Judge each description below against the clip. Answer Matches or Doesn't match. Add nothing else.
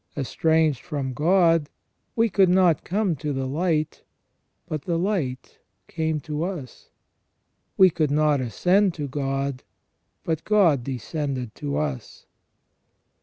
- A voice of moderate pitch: Matches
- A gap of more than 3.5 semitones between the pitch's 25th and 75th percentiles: Matches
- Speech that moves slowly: Matches